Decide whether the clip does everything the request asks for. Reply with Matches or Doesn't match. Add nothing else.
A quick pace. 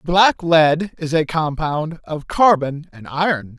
Doesn't match